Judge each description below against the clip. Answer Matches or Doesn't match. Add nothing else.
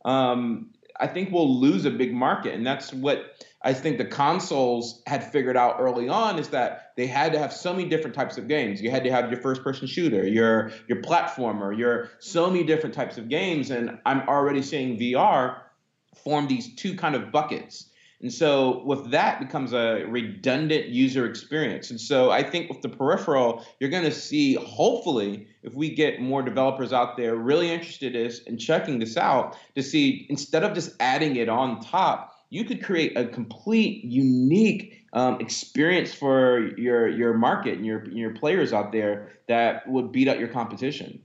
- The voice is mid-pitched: Doesn't match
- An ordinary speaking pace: Matches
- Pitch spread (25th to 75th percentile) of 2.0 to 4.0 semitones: Doesn't match